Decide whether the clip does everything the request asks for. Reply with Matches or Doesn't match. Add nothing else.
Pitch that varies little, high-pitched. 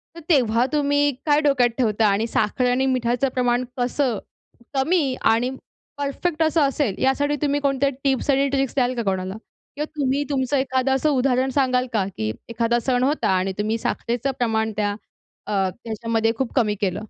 Doesn't match